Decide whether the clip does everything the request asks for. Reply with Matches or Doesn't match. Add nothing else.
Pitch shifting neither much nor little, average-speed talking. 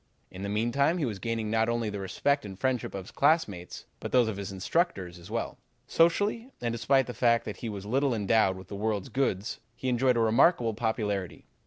Doesn't match